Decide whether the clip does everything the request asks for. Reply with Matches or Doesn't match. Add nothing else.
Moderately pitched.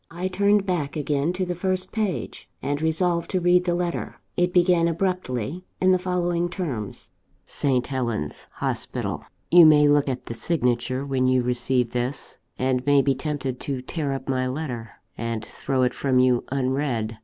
Matches